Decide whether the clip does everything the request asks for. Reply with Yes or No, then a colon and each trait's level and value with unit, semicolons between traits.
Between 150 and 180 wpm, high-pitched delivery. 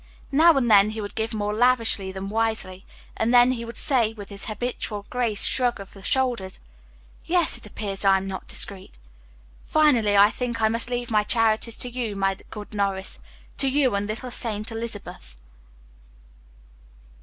Yes: average, 170 wpm; high, 220 Hz